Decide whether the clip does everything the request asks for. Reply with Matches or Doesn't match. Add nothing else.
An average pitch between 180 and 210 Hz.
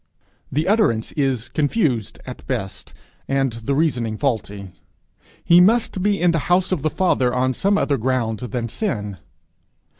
Doesn't match